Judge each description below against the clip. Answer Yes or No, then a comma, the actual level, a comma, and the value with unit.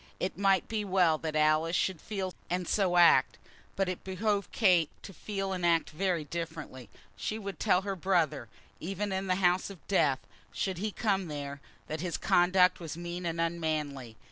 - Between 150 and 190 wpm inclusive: Yes, average, 185 wpm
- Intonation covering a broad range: No, average, 3.1 semitones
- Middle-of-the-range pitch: Yes, medium, 180 Hz